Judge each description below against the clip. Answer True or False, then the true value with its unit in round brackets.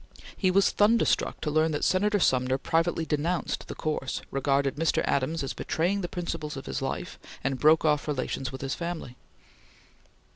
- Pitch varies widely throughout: False (4.0 semitones)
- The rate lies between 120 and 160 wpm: False (170 wpm)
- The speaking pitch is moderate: True (155 Hz)